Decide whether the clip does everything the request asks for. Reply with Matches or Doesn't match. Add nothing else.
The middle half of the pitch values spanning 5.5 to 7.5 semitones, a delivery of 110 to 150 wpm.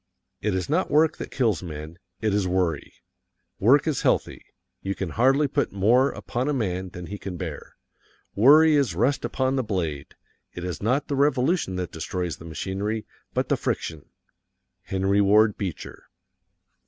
Doesn't match